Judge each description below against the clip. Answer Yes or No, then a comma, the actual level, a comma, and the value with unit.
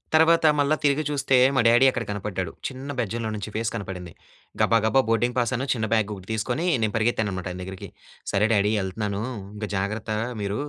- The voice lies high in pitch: No, low, 110 Hz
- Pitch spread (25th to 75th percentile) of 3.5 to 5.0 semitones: Yes, average, 3.8 semitones